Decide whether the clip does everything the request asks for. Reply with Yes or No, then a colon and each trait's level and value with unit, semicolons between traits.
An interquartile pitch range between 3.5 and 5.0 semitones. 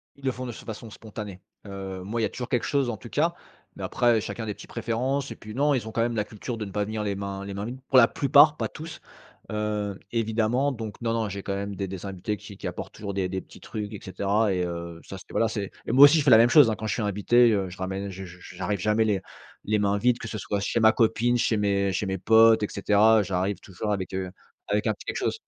No: average, 2.9 semitones